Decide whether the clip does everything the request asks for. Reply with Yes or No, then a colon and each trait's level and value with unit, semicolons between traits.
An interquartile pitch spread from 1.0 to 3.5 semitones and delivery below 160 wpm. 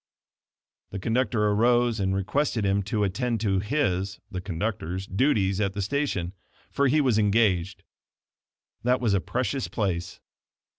No: average, 4.2 semitones; average, 140 wpm